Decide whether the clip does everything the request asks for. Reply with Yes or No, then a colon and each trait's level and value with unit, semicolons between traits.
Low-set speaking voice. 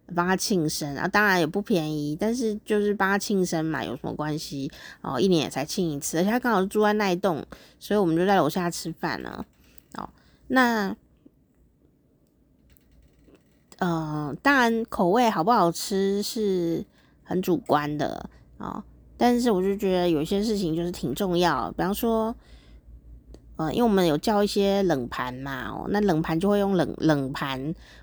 No: medium, 180 Hz